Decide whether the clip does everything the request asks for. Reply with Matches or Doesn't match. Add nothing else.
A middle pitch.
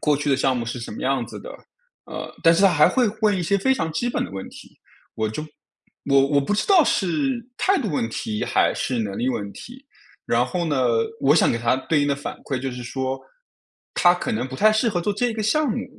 Matches